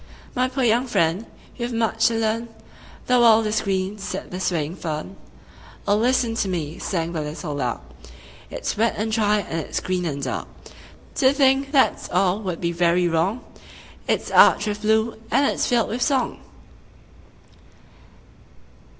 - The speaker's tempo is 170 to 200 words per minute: No, average, 160 wpm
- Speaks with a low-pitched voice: No, high, 210 Hz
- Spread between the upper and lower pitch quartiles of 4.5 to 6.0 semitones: Yes, average, 5.1 semitones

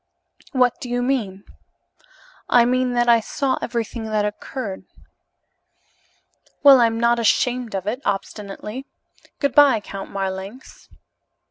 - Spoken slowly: Yes, slow, 120 wpm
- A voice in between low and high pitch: No, high, 235 Hz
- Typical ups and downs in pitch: Yes, average, 3.4 semitones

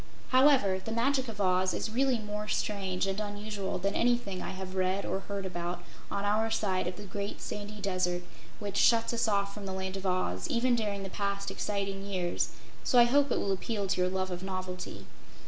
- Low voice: No, high, 200 Hz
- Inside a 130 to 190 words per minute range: No, fast, 205 wpm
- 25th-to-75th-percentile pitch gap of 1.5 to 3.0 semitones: Yes, narrow, 2.5 semitones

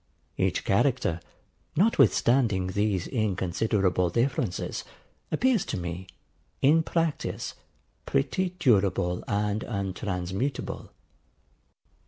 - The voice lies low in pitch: Yes, low, 105 Hz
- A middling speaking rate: No, slow, 75 wpm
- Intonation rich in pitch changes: Yes, wide, 6.4 semitones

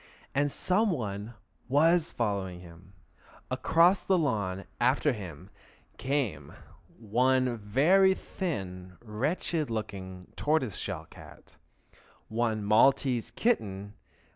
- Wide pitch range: Yes, wide, 6.8 semitones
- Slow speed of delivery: Yes, slow, 100 wpm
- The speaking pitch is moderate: No, low, 115 Hz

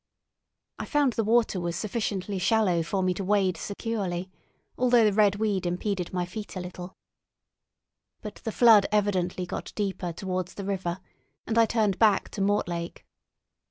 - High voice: Yes, high, 195 Hz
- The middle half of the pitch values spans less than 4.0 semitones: Yes, average, 3.0 semitones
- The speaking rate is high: No, average, 160 wpm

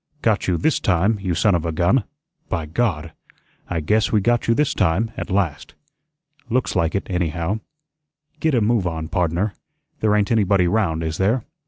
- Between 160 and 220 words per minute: Yes, average, 180 wpm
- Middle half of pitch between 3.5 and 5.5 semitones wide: Yes, average, 4.7 semitones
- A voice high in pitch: No, very low, 95 Hz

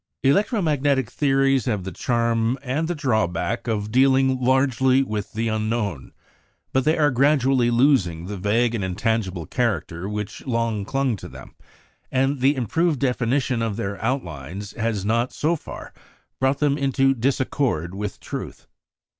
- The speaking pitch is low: Yes, low, 120 Hz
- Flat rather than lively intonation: No, average, 4.3 semitones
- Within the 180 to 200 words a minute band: No, average, 145 wpm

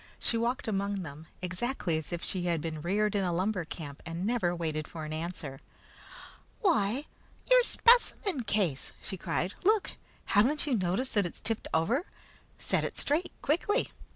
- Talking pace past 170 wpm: No, average, 165 wpm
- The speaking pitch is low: No, high, 195 Hz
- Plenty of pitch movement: Yes, wide, 6.8 semitones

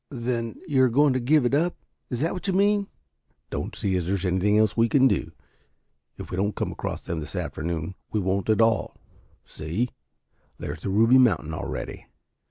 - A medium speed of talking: Yes, average, 195 wpm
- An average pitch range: No, wide, 5.8 semitones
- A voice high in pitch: No, low, 115 Hz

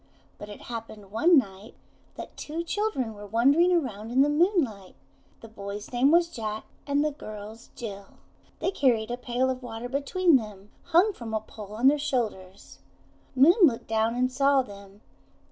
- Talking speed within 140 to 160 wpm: No, average, 170 wpm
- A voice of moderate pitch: No, high, 240 Hz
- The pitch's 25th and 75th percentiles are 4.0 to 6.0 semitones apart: Yes, average, 5.2 semitones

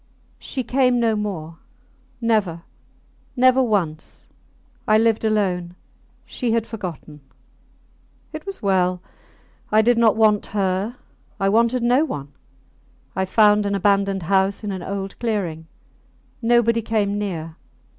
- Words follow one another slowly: Yes, slow, 125 wpm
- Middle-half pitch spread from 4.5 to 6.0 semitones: No, average, 3.5 semitones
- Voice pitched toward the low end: No, high, 210 Hz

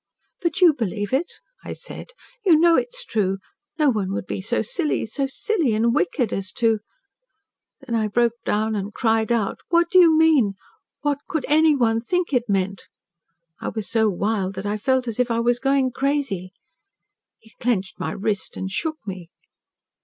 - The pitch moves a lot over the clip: Yes, wide, 6.5 semitones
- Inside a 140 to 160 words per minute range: No, average, 185 wpm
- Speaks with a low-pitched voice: No, high, 235 Hz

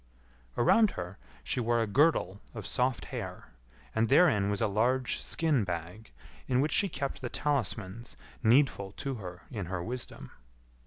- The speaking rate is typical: Yes, average, 155 wpm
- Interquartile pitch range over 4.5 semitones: Yes, average, 5.2 semitones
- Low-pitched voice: Yes, low, 115 Hz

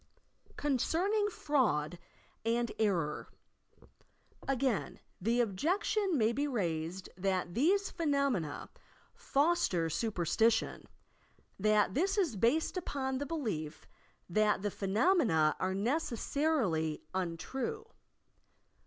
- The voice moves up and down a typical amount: No, wide, 8.0 semitones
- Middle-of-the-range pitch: No, high, 230 Hz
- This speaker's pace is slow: Yes, slow, 90 wpm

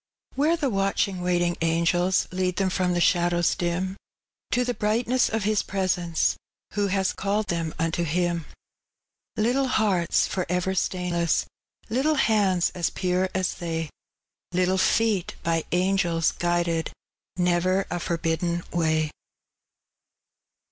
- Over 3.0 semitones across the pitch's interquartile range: No, narrow, 2.5 semitones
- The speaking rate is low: Yes, slow, 125 wpm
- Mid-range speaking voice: Yes, medium, 180 Hz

